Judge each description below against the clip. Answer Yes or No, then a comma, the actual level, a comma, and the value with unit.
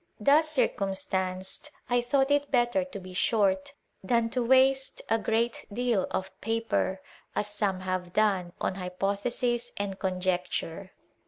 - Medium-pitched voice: No, high, 210 Hz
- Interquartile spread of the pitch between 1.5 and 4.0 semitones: No, average, 4.5 semitones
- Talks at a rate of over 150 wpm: No, slow, 135 wpm